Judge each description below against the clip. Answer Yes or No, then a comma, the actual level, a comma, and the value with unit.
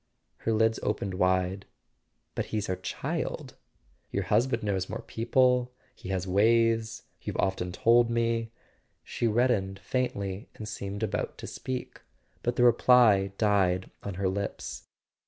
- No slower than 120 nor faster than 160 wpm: Yes, average, 140 wpm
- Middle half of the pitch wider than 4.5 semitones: No, average, 3.4 semitones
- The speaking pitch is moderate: No, low, 110 Hz